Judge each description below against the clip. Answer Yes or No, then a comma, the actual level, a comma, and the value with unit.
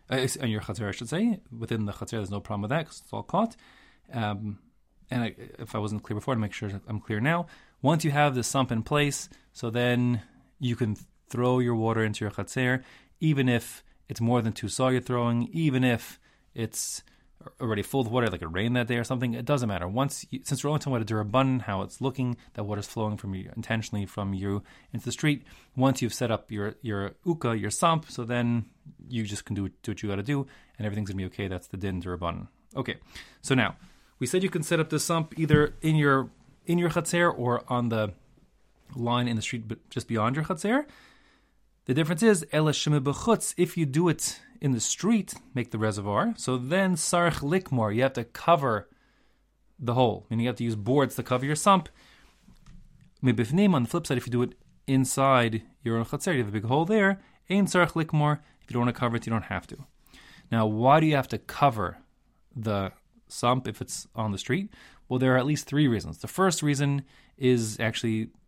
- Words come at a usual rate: No, fast, 220 wpm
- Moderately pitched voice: No, low, 125 Hz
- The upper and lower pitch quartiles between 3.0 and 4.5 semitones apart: No, average, 5.1 semitones